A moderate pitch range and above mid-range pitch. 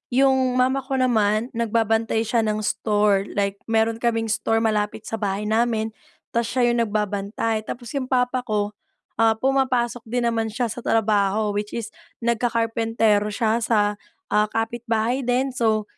No: narrow, 2.1 semitones; high, 225 Hz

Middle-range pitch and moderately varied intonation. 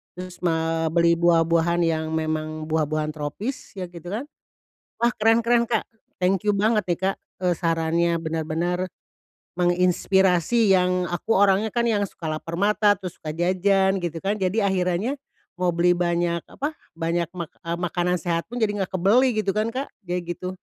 Yes: medium, 180 Hz; average, 3.2 semitones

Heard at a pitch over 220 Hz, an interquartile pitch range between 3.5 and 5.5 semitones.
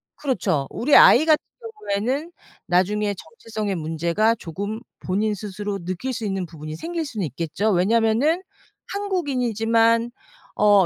No: high, 210 Hz; average, 4.7 semitones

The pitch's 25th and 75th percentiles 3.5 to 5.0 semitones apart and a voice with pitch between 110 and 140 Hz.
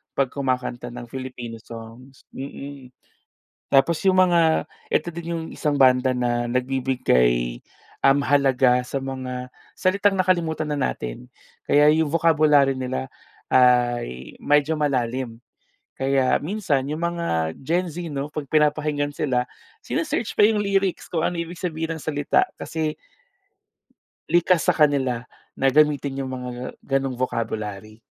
Yes: average, 4.1 semitones; low, 135 Hz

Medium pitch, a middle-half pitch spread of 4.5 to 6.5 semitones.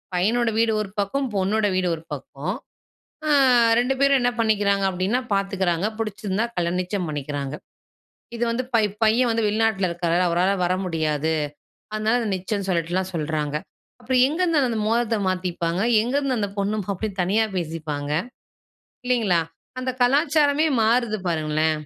No: high, 200 Hz; average, 5.1 semitones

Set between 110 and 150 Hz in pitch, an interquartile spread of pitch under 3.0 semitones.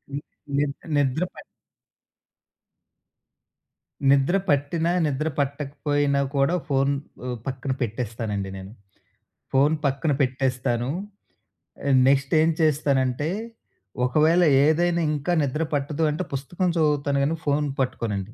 Yes: medium, 140 Hz; narrow, 2.5 semitones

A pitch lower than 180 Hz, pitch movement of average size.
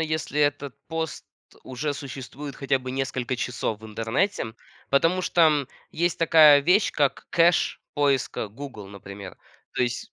Yes: medium, 140 Hz; average, 4.1 semitones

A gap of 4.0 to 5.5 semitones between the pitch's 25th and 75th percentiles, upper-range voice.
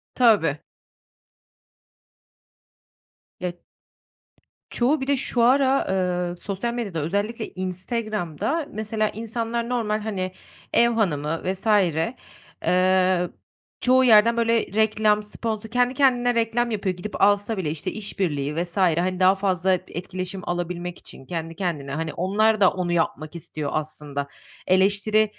Yes: average, 4.3 semitones; high, 195 Hz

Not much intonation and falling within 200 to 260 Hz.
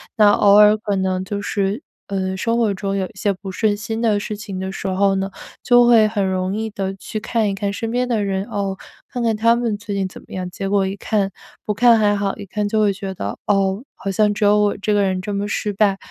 Yes: narrow, 1.7 semitones; high, 205 Hz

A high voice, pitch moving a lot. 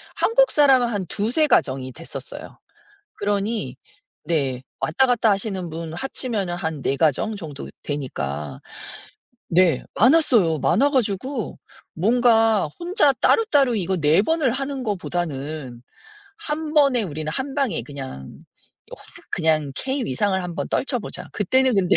Yes: high, 200 Hz; wide, 8.7 semitones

